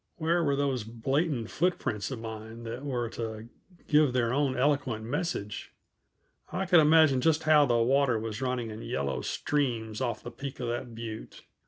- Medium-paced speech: Yes, average, 170 wpm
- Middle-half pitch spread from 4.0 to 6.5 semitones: Yes, average, 4.3 semitones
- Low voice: Yes, low, 125 Hz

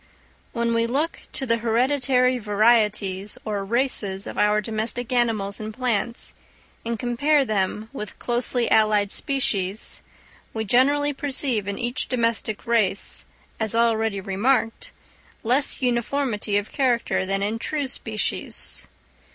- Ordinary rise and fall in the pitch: Yes, average, 3.2 semitones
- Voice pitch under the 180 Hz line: No, high, 230 Hz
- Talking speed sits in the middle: No, slow, 125 wpm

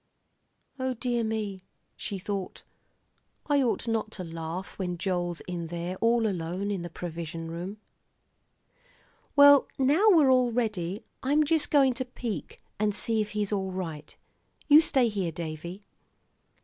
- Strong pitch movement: Yes, wide, 6.0 semitones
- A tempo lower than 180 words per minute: Yes, average, 145 wpm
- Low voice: No, high, 205 Hz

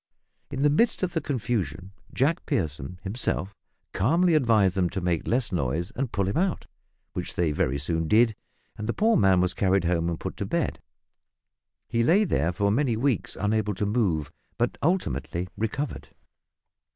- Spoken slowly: No, average, 170 wpm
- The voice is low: Yes, low, 105 Hz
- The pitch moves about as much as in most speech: No, wide, 7.0 semitones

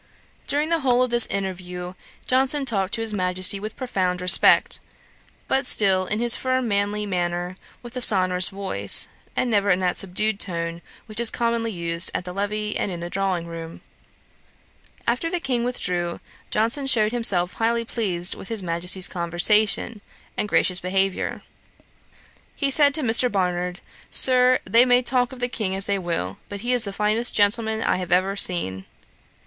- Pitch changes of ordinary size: Yes, average, 4.7 semitones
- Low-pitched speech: No, high, 200 Hz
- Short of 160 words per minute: No, average, 170 wpm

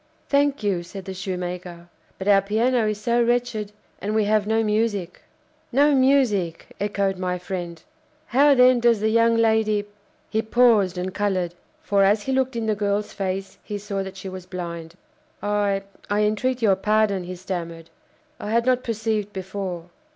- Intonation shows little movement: No, average, 3.3 semitones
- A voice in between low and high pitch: No, high, 205 Hz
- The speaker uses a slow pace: No, average, 175 wpm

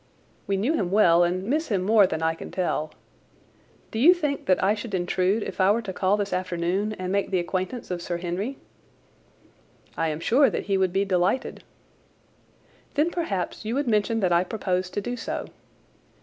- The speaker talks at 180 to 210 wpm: Yes, average, 190 wpm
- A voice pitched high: Yes, high, 195 Hz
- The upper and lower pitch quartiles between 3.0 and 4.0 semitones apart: Yes, average, 3.5 semitones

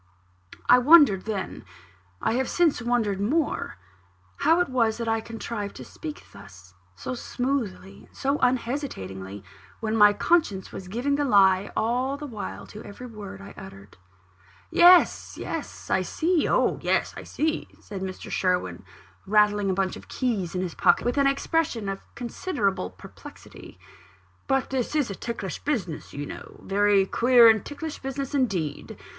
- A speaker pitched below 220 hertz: No, high, 225 Hz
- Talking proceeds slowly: No, average, 160 wpm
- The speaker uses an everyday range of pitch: No, wide, 5.7 semitones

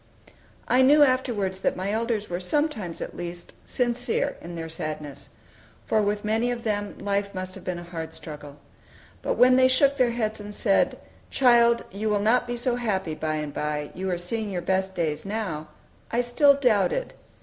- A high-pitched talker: Yes, high, 205 Hz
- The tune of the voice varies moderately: No, wide, 5.7 semitones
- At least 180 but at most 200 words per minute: Yes, average, 185 wpm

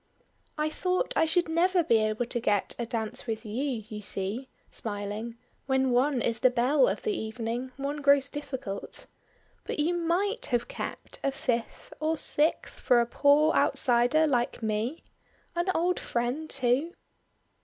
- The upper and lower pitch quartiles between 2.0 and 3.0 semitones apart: No, average, 5.1 semitones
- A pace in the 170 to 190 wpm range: No, average, 155 wpm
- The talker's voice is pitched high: Yes, very high, 260 Hz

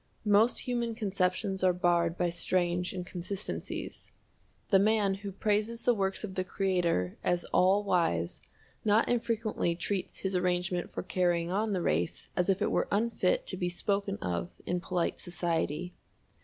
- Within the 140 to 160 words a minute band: Yes, average, 155 wpm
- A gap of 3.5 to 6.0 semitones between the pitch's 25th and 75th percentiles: No, average, 2.8 semitones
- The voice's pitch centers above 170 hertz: Yes, medium, 185 Hz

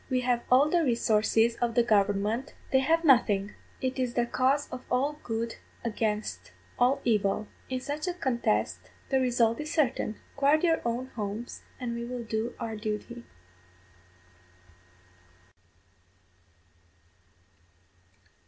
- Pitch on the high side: Yes, high, 240 Hz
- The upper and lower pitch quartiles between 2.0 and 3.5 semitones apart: Yes, average, 3.0 semitones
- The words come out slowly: Yes, slow, 125 wpm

